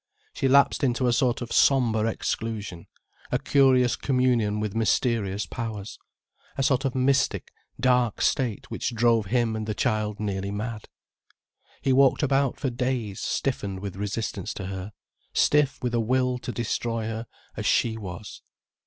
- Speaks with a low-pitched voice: Yes, low, 115 Hz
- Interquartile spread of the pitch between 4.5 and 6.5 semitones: No, average, 3.3 semitones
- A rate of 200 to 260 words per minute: No, average, 155 wpm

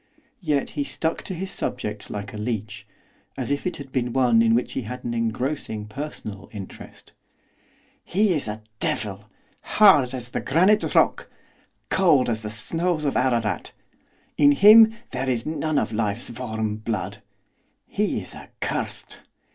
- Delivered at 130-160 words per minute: Yes, average, 155 wpm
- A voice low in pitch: Yes, low, 125 Hz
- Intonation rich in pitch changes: Yes, wide, 5.7 semitones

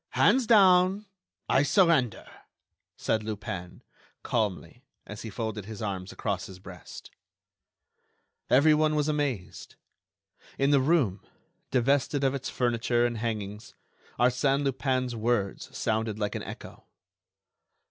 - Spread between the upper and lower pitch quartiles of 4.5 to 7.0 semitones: Yes, average, 5.2 semitones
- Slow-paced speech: Yes, slow, 115 wpm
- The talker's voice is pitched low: Yes, low, 120 Hz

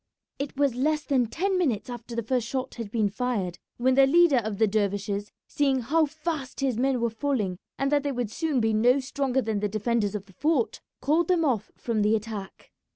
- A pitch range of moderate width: Yes, average, 4.5 semitones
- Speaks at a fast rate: Yes, fast, 215 wpm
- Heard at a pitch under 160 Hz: No, high, 245 Hz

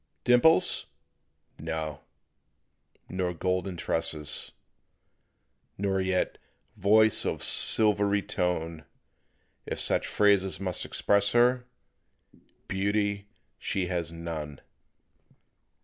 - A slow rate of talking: Yes, slow, 80 wpm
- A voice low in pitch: Yes, very low, 95 Hz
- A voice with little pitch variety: No, average, 3.5 semitones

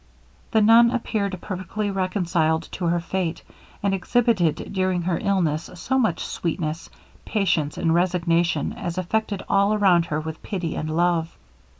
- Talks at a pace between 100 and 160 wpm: Yes, average, 140 wpm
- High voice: No, medium, 180 Hz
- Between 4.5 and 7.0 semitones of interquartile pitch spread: No, average, 3.1 semitones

